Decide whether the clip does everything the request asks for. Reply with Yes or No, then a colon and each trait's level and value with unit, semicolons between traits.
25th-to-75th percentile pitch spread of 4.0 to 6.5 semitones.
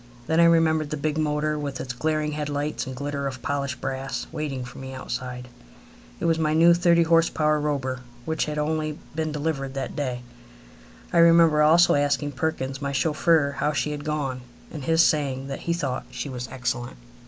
No: average, 2.7 semitones